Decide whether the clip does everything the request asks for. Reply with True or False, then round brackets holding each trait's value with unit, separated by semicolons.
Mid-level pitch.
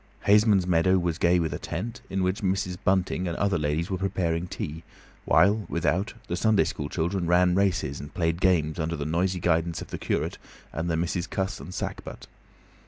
False (90 Hz)